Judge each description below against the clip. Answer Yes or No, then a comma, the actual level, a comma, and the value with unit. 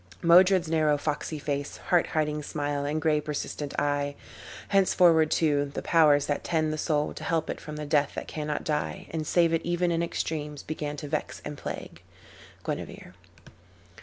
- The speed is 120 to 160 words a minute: No, average, 170 wpm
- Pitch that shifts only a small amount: Yes, narrow, 1.9 semitones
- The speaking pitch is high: No, medium, 150 Hz